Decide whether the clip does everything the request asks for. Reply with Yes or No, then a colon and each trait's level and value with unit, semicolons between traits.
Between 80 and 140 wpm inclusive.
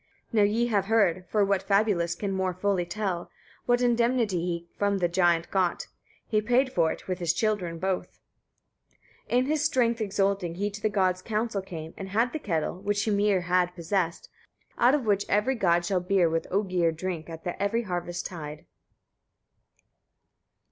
No: average, 175 wpm